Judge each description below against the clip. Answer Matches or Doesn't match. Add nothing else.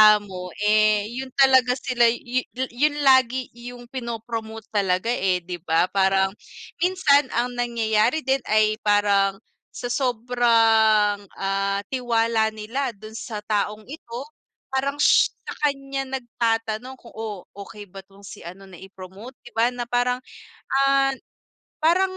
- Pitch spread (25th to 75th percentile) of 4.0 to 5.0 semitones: Doesn't match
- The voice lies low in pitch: Doesn't match